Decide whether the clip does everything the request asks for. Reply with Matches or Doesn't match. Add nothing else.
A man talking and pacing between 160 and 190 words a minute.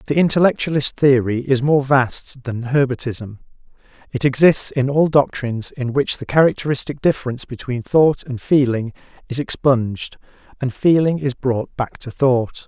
Doesn't match